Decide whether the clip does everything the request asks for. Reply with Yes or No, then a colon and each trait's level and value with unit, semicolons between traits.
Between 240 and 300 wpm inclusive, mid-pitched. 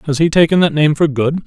Yes: fast, 285 wpm; medium, 155 Hz